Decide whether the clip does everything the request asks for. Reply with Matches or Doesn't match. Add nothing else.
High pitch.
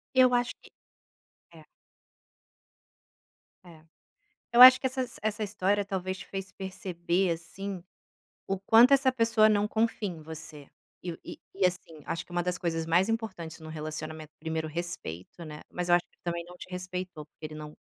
Doesn't match